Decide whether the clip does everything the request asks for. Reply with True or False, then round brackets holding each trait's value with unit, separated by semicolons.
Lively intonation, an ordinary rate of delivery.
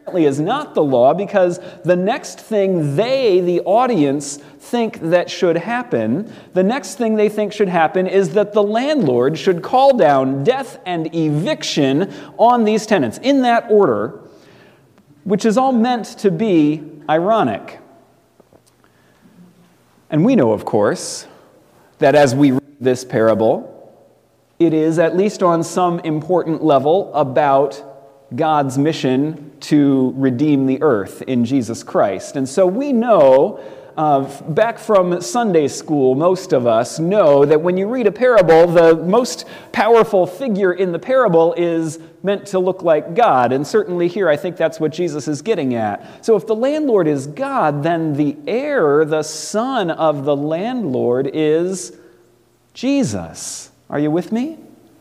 True (6.1 semitones; 150 wpm)